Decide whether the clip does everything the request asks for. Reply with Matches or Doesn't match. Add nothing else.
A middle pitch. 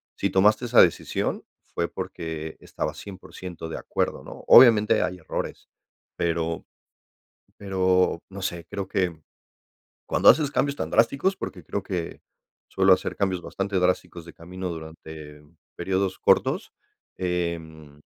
Doesn't match